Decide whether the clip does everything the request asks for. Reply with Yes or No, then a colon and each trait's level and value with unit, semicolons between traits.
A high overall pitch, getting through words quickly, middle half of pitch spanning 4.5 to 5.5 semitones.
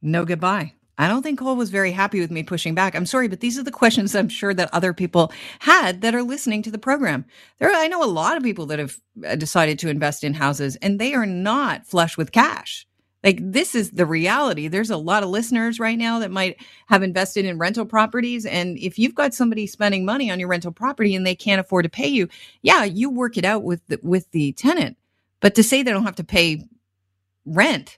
Yes: high, 195 Hz; fast, 235 wpm; average, 5.0 semitones